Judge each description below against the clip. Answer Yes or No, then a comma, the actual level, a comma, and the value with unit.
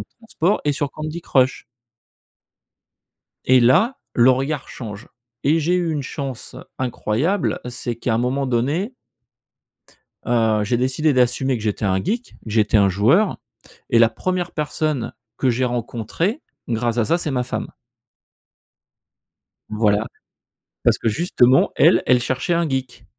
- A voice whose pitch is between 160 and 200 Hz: No, low, 130 Hz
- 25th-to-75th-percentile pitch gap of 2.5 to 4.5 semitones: No, average, 4.9 semitones